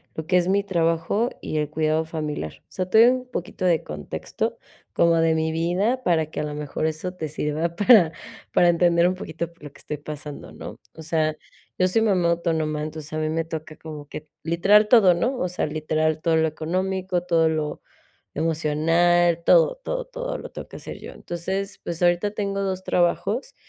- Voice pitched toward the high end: No, medium, 170 Hz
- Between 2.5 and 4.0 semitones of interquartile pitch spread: Yes, average, 3.0 semitones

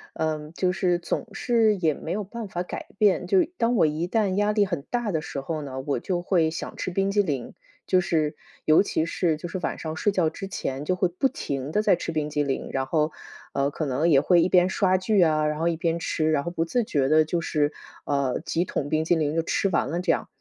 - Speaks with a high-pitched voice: No, medium, 165 Hz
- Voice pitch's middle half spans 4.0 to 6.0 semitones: No, average, 3.6 semitones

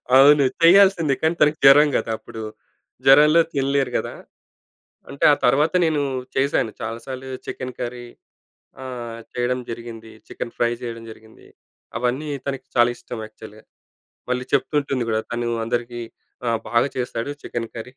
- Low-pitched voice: Yes, low, 125 Hz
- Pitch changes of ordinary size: Yes, average, 3.0 semitones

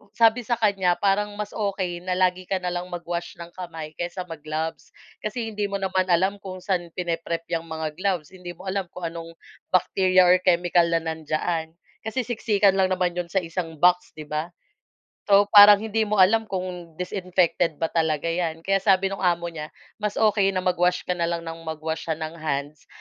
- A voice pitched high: No, medium, 180 Hz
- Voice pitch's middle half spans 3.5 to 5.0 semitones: No, average, 2.7 semitones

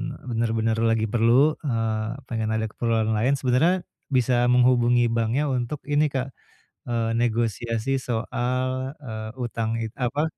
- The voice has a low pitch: Yes, low, 120 Hz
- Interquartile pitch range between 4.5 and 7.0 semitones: No, narrow, 2.4 semitones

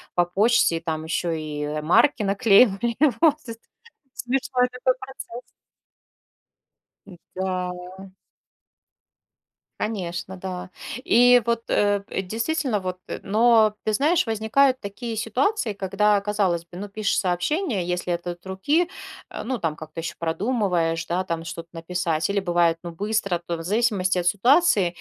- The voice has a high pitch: Yes, high, 195 Hz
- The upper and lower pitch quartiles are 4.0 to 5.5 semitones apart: Yes, average, 4.8 semitones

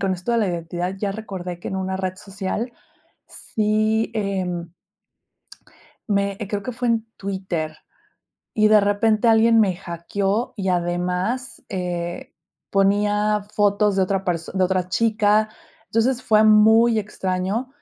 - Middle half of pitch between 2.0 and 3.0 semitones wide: Yes, average, 2.7 semitones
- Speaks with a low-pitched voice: No, high, 200 Hz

